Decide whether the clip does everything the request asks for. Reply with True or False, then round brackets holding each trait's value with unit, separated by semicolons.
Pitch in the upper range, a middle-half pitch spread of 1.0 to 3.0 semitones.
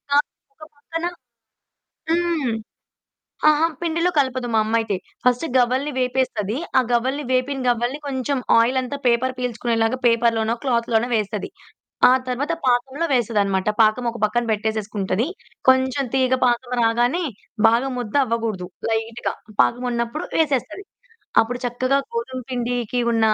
True (245 Hz; 2.5 semitones)